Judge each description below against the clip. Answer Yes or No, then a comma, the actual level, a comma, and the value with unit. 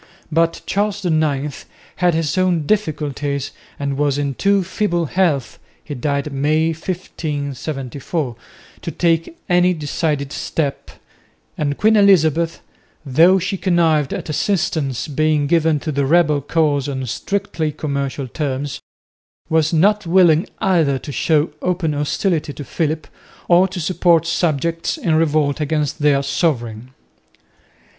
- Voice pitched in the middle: Yes, medium, 155 Hz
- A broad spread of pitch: No, average, 3.3 semitones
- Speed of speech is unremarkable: No, slow, 125 wpm